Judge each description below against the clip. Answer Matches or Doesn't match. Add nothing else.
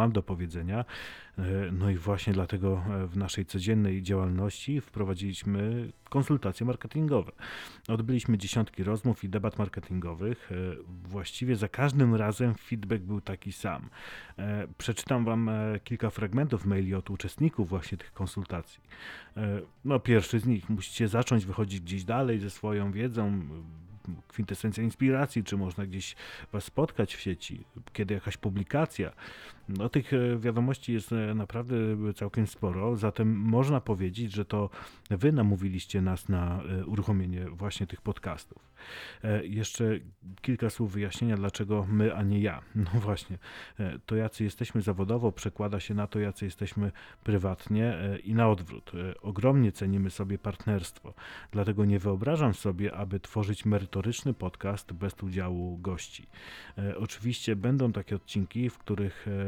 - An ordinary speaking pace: Matches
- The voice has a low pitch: Matches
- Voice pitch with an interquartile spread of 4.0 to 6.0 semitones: Doesn't match